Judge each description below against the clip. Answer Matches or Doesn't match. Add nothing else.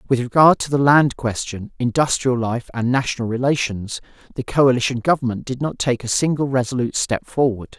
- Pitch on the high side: Doesn't match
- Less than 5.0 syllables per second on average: Doesn't match